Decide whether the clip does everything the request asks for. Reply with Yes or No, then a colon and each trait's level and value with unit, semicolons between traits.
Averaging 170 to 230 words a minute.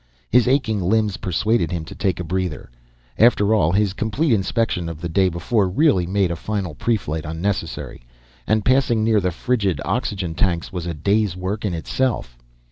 Yes: average, 175 wpm